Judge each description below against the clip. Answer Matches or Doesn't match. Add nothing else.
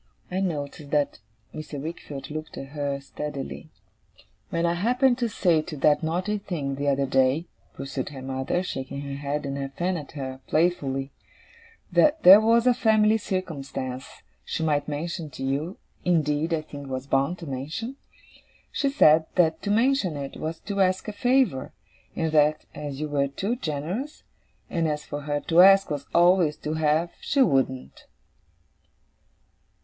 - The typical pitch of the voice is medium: Matches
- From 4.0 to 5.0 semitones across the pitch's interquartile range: Matches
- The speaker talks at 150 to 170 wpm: Matches